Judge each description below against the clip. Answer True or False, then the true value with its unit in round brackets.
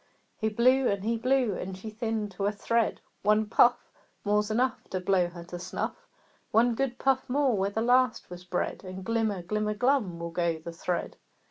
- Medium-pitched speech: False (210 Hz)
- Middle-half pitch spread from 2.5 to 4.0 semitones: False (4.4 semitones)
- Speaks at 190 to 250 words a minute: True (195 wpm)